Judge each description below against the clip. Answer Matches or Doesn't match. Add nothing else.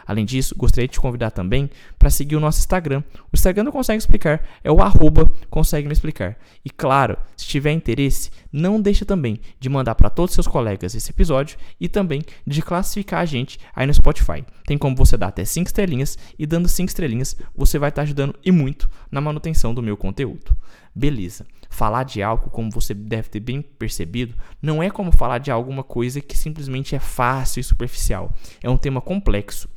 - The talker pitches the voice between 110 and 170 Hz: Matches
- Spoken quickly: Matches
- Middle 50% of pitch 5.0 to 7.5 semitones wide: Matches